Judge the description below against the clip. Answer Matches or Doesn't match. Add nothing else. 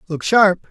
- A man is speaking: Matches